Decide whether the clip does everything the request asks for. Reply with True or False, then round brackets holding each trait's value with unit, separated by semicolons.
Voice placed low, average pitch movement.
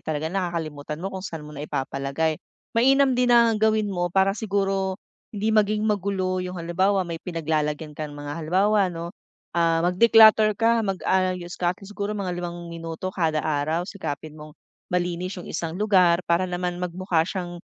False (180 Hz; 3.4 semitones)